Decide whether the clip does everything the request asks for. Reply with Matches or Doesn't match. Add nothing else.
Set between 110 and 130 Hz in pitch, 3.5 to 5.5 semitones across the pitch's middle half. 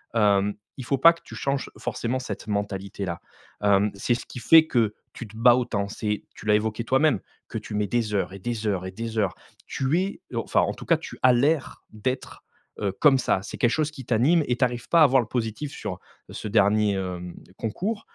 Matches